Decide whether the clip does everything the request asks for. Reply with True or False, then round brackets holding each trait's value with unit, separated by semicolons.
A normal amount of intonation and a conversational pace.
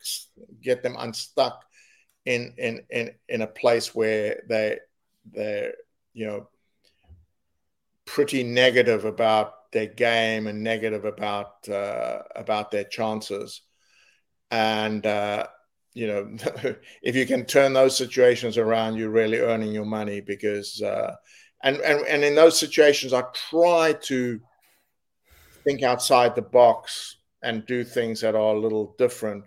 False (3.3 semitones; 130 wpm)